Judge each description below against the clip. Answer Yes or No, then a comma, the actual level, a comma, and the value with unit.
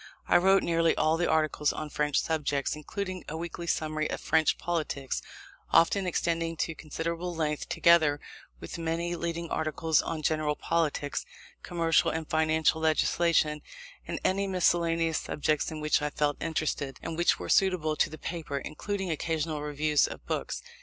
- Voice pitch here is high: No, medium, 160 Hz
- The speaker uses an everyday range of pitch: No, narrow, 1.8 semitones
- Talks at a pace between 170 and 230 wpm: No, average, 155 wpm